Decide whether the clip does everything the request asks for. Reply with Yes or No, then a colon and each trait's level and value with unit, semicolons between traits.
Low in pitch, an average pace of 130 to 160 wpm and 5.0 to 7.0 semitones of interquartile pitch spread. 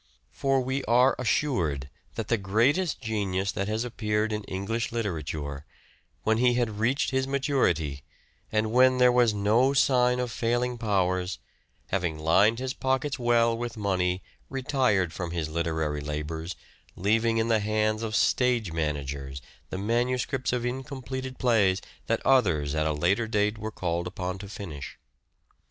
Yes: low, 110 Hz; average, 150 wpm; wide, 5.6 semitones